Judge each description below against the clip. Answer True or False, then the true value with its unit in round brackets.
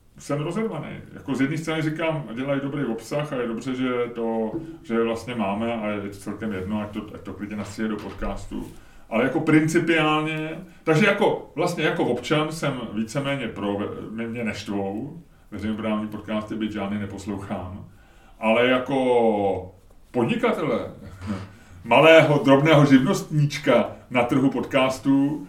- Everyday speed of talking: True (135 wpm)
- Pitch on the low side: True (120 Hz)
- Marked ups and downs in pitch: True (6.3 semitones)